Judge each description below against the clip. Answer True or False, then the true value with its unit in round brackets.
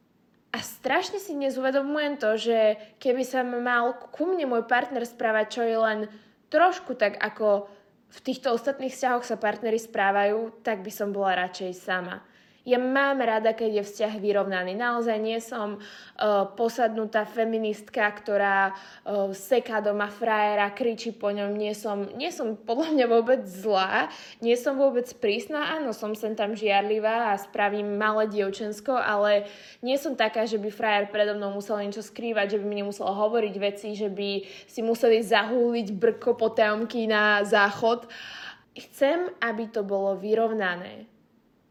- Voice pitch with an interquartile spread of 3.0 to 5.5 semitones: False (2.6 semitones)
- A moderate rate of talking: True (150 wpm)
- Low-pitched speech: False (220 Hz)